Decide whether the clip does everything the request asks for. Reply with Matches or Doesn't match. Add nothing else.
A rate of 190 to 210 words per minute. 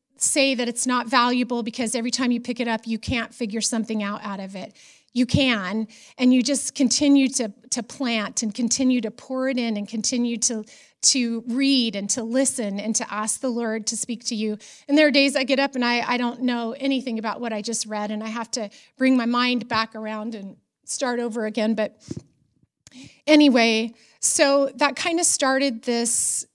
Matches